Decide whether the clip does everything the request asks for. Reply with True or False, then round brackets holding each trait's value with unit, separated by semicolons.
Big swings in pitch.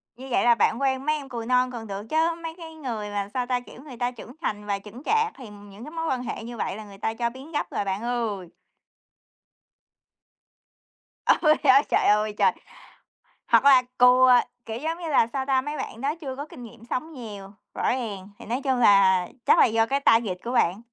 False (4.3 semitones)